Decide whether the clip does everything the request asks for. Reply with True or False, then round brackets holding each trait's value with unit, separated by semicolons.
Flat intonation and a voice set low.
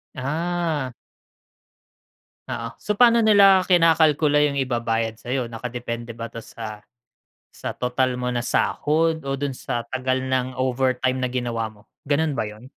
False (4.1 semitones; 130 Hz)